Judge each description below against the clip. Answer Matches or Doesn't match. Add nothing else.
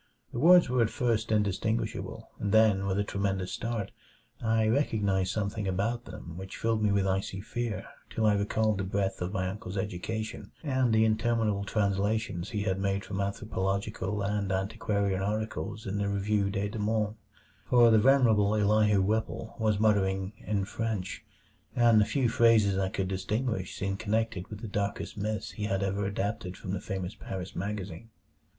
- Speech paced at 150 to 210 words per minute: Matches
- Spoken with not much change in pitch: Matches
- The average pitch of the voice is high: Doesn't match